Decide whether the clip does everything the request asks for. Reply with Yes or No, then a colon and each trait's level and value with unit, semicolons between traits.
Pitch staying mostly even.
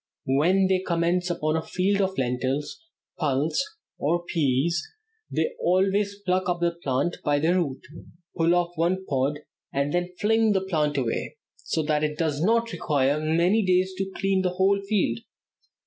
No: average, 4.0 semitones